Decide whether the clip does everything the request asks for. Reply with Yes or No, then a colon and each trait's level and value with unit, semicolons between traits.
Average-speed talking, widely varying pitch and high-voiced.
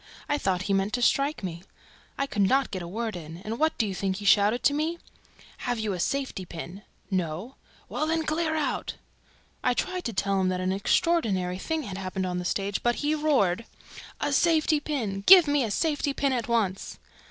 No: fast, 210 wpm; wide, 7.4 semitones; high, 220 Hz